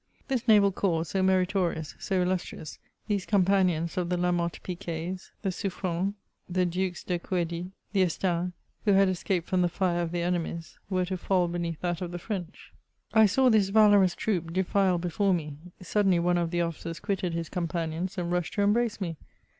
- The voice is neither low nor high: Yes, medium, 180 Hz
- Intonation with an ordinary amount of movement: No, narrow, 2.2 semitones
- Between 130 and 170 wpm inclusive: No, average, 185 wpm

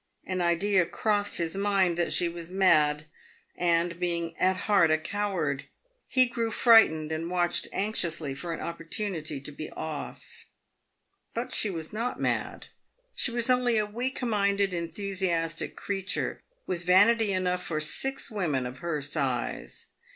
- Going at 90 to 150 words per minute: Yes, average, 145 wpm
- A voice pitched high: No, medium, 180 Hz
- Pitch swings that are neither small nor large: Yes, average, 3.9 semitones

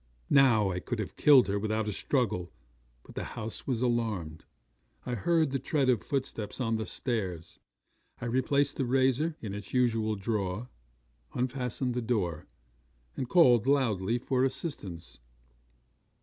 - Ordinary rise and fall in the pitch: Yes, average, 4.0 semitones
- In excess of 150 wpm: No, average, 145 wpm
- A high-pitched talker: No, low, 120 Hz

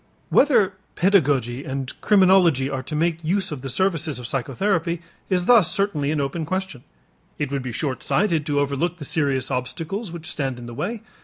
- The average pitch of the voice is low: No, medium, 155 Hz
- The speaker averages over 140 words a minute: Yes, average, 180 wpm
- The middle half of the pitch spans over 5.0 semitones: Yes, wide, 5.6 semitones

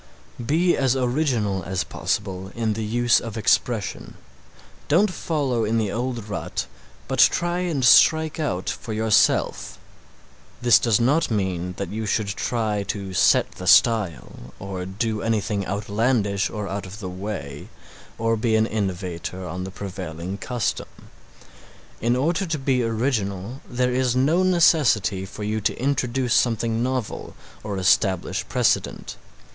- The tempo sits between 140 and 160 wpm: Yes, average, 145 wpm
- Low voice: Yes, low, 110 Hz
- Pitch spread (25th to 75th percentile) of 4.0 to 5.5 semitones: Yes, average, 4.4 semitones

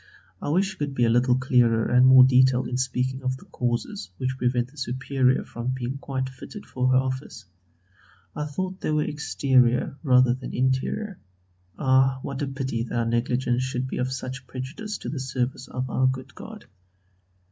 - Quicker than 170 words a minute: Yes, average, 185 wpm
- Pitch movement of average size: No, narrow, 1.4 semitones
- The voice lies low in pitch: Yes, low, 130 Hz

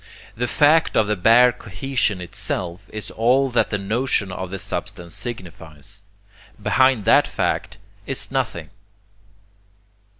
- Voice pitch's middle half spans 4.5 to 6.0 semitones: Yes, average, 5.0 semitones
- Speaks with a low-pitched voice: Yes, low, 105 Hz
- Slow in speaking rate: Yes, slow, 125 wpm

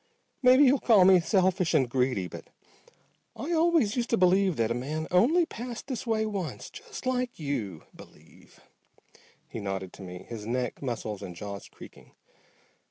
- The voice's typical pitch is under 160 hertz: No, medium, 180 Hz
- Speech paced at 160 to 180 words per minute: Yes, average, 165 wpm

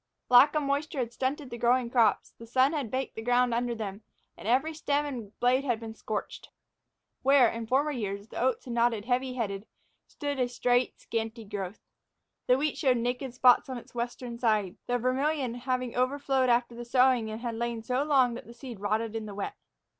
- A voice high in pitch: Yes, high, 245 Hz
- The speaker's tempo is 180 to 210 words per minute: Yes, average, 200 wpm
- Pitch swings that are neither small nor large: No, narrow, 2.3 semitones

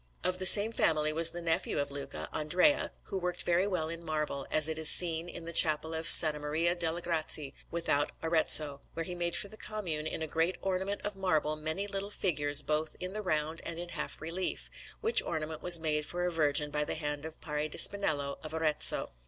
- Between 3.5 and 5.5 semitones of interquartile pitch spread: No, average, 2.7 semitones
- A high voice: No, medium, 160 Hz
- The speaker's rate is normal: No, fast, 215 wpm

